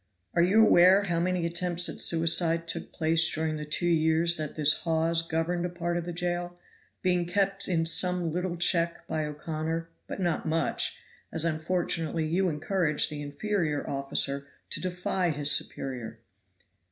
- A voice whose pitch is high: No, medium, 165 Hz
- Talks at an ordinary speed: Yes, average, 160 wpm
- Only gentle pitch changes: Yes, narrow, 2.0 semitones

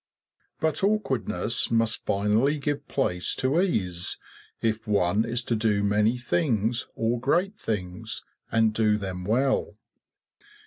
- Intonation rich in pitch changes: No, average, 4.2 semitones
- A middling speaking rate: No, slow, 125 wpm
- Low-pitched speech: Yes, low, 115 Hz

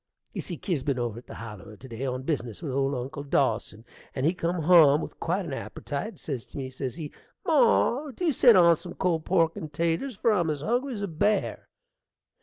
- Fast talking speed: Yes, fast, 215 wpm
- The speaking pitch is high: No, medium, 155 Hz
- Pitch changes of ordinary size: No, wide, 5.9 semitones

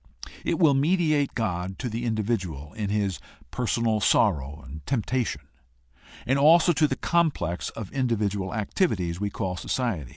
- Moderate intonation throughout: No, wide, 6.3 semitones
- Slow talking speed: No, average, 150 wpm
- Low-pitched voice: Yes, low, 110 Hz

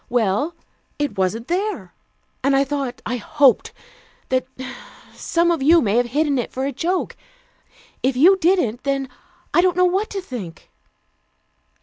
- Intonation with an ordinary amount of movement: No, wide, 5.8 semitones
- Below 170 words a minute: Yes, average, 150 wpm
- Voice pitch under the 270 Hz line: No, very high, 275 Hz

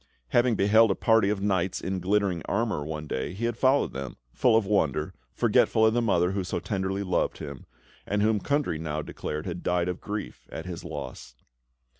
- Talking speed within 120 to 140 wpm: No, average, 195 wpm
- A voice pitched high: No, very low, 95 Hz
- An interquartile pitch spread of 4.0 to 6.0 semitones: Yes, average, 4.4 semitones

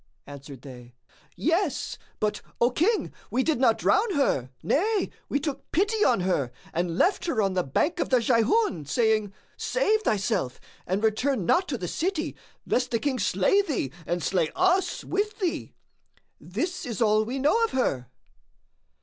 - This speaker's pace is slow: No, average, 160 wpm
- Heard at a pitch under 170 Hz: No, high, 245 Hz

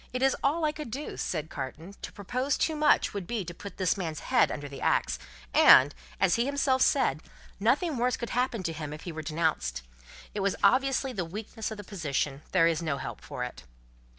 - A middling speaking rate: No, fast, 215 wpm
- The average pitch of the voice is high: Yes, high, 195 Hz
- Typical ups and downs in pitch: No, wide, 8.2 semitones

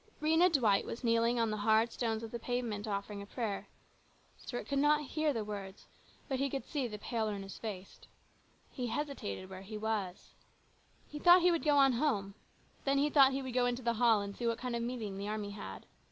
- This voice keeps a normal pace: No, fast, 225 wpm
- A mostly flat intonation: No, average, 4.6 semitones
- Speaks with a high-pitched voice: Yes, high, 235 Hz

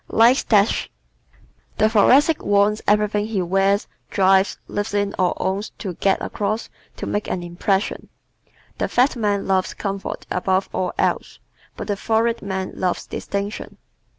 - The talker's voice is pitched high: Yes, high, 200 Hz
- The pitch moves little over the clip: Yes, narrow, 1.9 semitones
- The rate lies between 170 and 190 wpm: No, average, 150 wpm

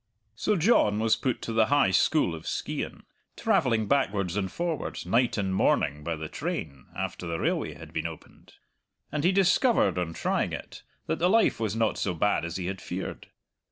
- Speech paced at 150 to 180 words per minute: No, average, 190 wpm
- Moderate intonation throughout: No, wide, 8.1 semitones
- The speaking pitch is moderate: No, low, 105 Hz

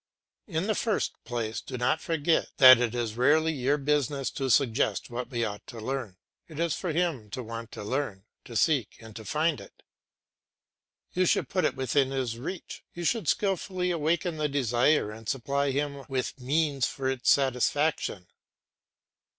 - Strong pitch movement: No, average, 4.7 semitones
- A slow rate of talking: No, average, 170 wpm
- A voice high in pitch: No, low, 135 Hz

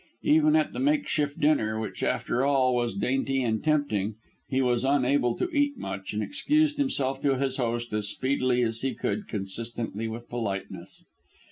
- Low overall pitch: Yes, low, 130 Hz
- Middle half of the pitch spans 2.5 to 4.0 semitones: No, average, 4.6 semitones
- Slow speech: No, average, 165 wpm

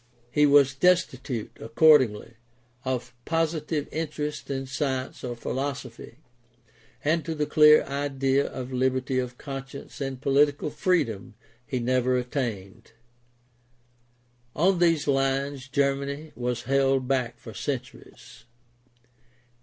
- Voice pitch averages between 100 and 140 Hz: Yes, low, 135 Hz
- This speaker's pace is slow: Yes, slow, 105 wpm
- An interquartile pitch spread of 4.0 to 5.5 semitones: No, narrow, 2.6 semitones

